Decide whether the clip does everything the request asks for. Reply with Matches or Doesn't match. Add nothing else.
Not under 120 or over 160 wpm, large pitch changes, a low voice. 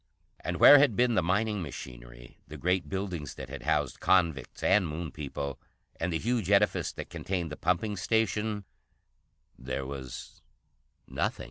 Matches